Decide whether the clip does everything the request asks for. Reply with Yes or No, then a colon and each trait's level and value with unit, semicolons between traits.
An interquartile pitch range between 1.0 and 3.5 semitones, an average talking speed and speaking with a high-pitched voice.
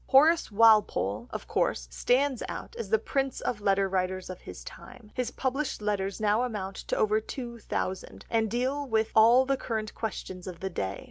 No: average, 4.4 semitones; average, 185 wpm; high, 220 Hz